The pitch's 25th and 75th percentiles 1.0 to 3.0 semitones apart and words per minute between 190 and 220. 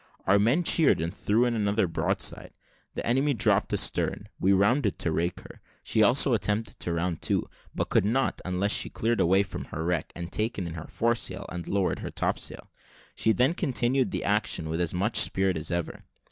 No: average, 5.0 semitones; average, 195 wpm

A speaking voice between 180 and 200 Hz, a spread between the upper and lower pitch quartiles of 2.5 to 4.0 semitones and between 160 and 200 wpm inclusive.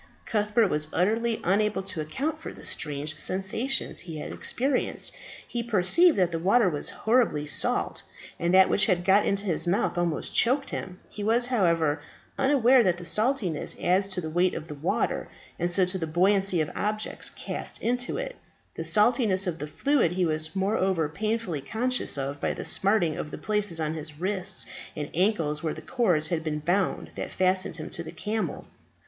No: medium, 185 Hz; average, 5.1 semitones; average, 180 wpm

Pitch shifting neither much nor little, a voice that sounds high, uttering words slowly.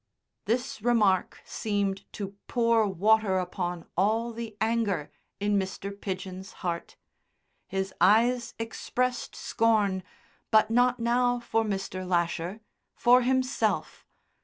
Yes: average, 3.5 semitones; high, 215 Hz; slow, 110 wpm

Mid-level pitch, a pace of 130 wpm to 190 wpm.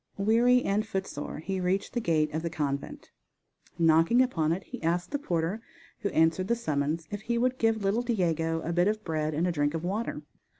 No: medium, 180 Hz; fast, 205 wpm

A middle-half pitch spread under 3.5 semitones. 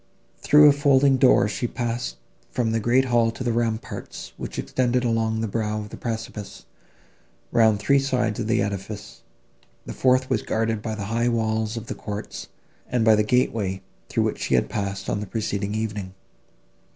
Yes: narrow, 2.5 semitones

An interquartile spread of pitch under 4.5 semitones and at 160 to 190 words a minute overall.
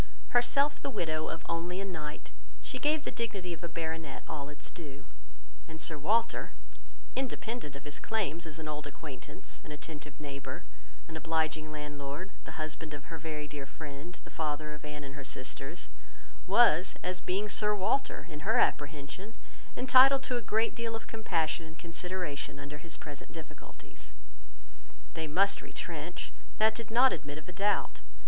No: average, 5.1 semitones; average, 170 wpm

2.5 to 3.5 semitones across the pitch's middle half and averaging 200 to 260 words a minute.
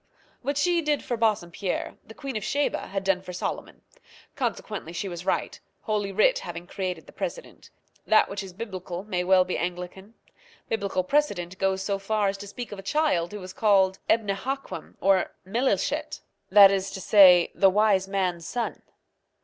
No: average, 2.9 semitones; average, 175 wpm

